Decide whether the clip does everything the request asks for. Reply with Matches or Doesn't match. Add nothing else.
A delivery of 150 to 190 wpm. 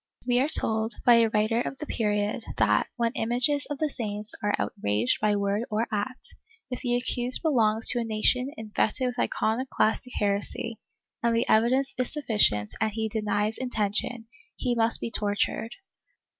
Matches